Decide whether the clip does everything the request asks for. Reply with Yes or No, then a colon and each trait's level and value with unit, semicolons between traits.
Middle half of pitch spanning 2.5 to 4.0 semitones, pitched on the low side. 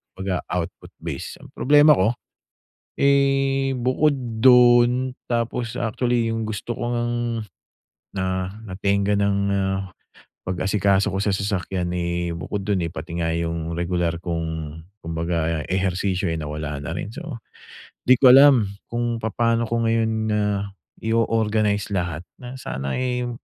No: average, 5.3 semitones; low, 105 Hz